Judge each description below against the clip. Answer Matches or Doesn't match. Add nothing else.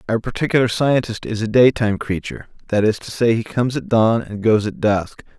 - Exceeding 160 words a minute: Matches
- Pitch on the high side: Doesn't match